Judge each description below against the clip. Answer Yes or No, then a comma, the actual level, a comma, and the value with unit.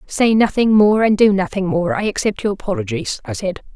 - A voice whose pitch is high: Yes, high, 195 Hz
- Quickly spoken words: Yes, fast, 210 wpm